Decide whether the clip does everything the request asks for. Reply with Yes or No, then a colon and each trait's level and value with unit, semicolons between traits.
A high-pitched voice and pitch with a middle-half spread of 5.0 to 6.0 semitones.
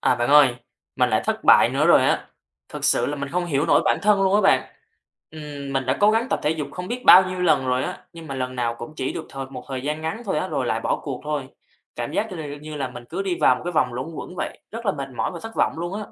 No: medium, 150 Hz; wide, 5.5 semitones